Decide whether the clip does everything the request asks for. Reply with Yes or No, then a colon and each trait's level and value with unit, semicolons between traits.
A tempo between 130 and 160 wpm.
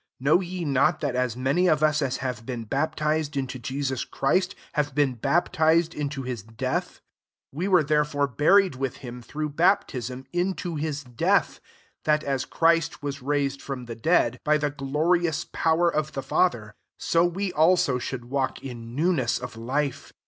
No: average, 175 wpm